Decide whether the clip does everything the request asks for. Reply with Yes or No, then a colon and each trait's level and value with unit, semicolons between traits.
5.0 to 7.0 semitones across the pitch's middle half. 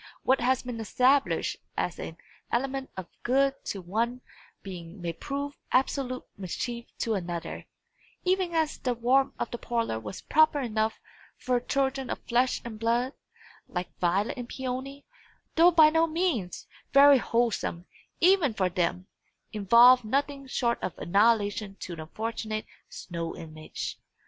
Yes: wide, 5.4 semitones